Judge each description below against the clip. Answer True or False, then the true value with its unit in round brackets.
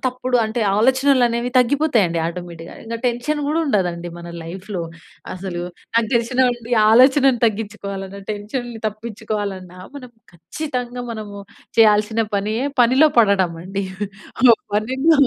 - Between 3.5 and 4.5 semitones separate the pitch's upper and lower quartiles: True (4.1 semitones)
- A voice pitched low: False (225 Hz)